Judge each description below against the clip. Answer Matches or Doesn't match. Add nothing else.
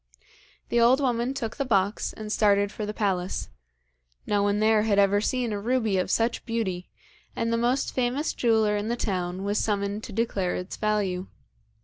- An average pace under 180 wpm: Doesn't match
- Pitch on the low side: Doesn't match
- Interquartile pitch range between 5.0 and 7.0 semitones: Doesn't match